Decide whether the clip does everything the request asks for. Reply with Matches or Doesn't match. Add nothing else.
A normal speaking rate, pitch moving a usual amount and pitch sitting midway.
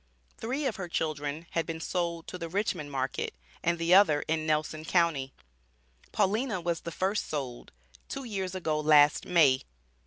Matches